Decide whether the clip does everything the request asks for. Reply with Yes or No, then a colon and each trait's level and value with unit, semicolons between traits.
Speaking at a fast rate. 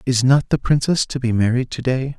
Yes: fast, 245 wpm